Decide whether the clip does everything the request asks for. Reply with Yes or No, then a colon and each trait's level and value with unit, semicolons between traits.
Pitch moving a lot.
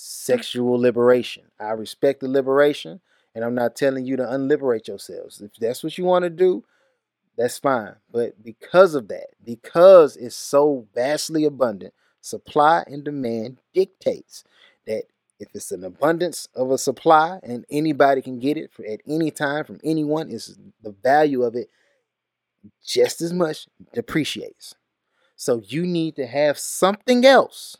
Yes: wide, 5.7 semitones